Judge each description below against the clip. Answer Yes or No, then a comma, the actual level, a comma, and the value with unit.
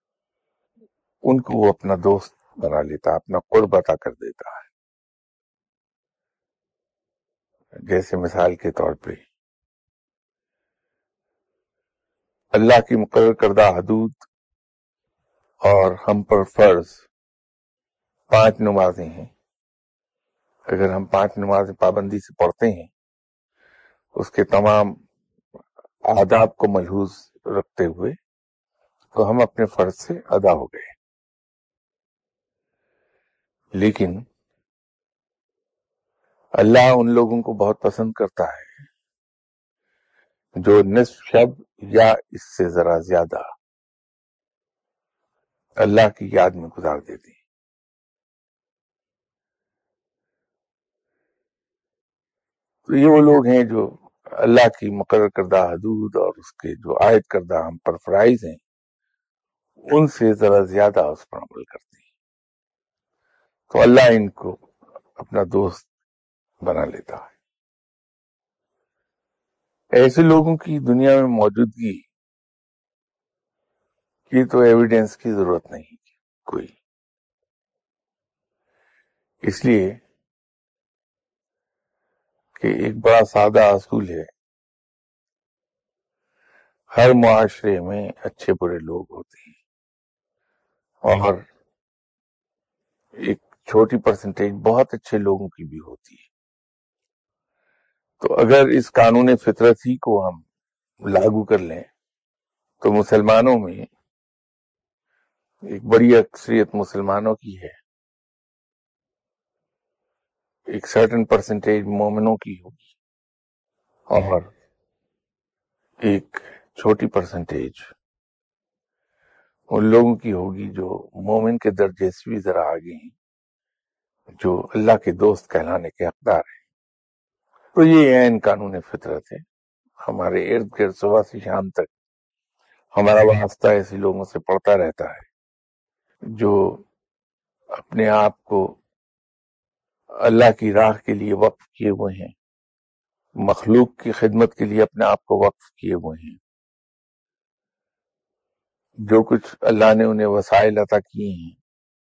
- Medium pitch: No, low, 110 Hz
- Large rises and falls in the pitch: No, average, 4.7 semitones